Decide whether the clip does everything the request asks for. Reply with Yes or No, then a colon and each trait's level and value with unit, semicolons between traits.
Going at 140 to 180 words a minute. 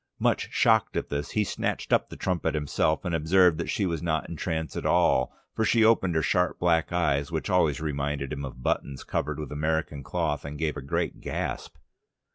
No: fast, 205 wpm